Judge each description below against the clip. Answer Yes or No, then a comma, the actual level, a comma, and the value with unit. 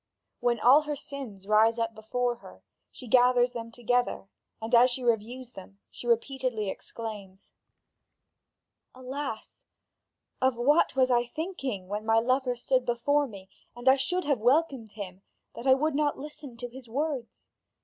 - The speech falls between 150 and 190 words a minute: Yes, average, 155 wpm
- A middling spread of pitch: Yes, average, 3.0 semitones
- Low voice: No, high, 245 Hz